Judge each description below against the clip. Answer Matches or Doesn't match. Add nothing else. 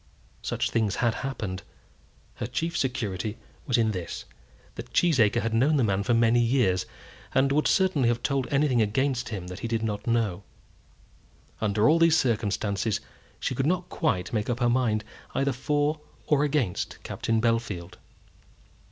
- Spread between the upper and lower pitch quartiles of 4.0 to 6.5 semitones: Matches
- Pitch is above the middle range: Doesn't match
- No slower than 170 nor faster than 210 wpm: Doesn't match